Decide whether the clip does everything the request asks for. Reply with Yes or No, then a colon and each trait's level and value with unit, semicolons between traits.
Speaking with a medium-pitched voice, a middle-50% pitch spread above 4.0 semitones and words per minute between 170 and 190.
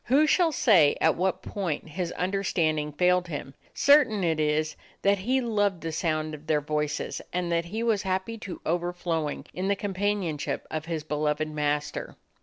Yes: medium, 175 Hz; average, 4.4 semitones; average, 175 wpm